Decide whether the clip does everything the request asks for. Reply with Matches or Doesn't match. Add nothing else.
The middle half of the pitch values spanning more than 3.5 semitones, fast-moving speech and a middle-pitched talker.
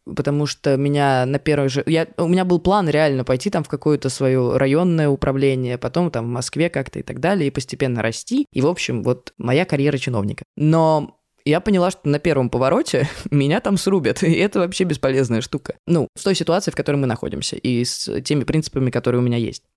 Matches